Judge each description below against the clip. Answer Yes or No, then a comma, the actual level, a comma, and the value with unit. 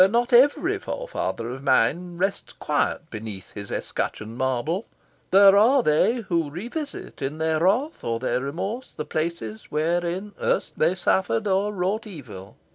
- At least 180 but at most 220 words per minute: No, average, 145 wpm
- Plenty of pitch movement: Yes, wide, 7.3 semitones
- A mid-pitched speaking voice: Yes, medium, 175 Hz